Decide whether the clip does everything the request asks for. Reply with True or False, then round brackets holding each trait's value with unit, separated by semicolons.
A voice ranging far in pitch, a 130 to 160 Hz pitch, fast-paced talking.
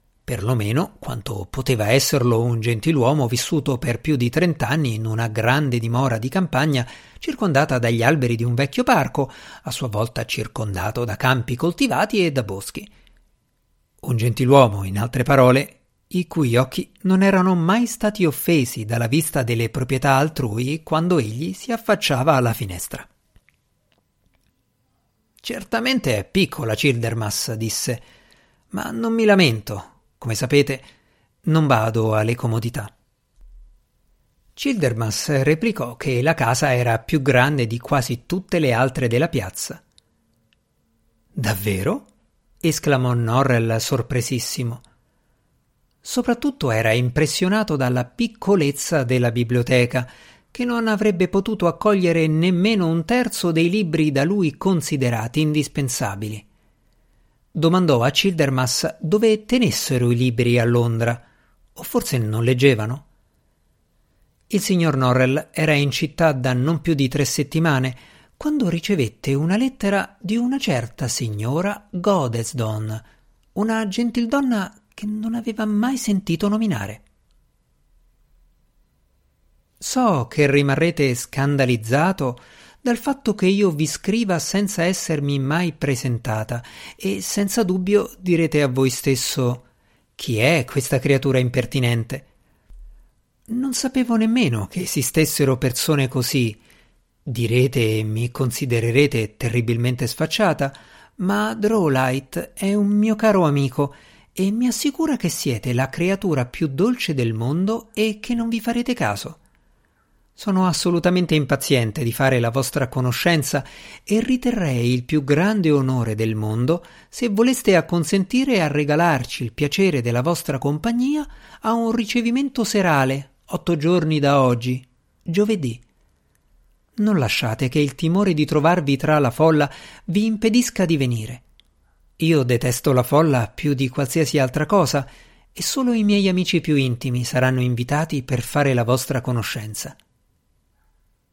False (7.1 semitones; 140 Hz; 125 wpm)